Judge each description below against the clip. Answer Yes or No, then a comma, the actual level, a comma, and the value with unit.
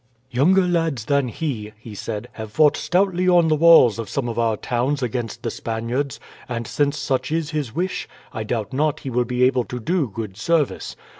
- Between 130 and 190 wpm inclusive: No, average, 200 wpm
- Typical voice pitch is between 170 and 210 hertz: No, low, 130 Hz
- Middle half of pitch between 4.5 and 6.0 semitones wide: Yes, average, 5.1 semitones